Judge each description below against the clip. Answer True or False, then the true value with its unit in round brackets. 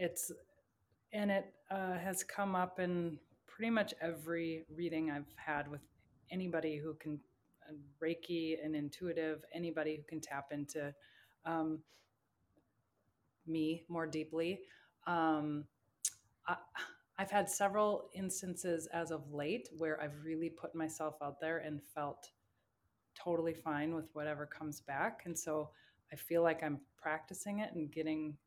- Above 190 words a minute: False (135 wpm)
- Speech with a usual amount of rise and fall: False (2.3 semitones)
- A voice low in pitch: False (160 Hz)